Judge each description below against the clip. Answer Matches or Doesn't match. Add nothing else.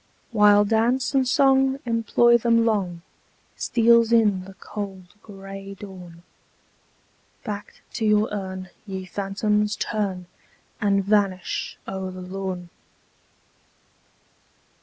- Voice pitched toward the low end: Doesn't match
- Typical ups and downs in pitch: Matches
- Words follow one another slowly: Matches